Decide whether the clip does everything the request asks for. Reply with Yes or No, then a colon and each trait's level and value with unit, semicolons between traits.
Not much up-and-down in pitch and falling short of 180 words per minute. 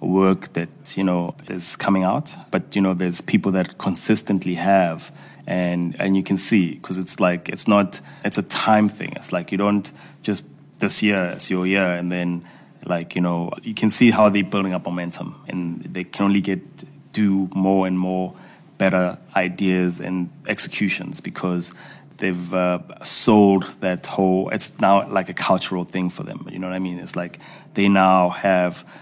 No: narrow, 1.9 semitones; average, 185 wpm